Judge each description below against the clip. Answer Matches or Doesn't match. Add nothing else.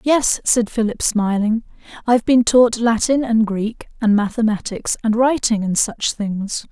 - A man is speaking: Doesn't match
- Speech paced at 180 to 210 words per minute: Doesn't match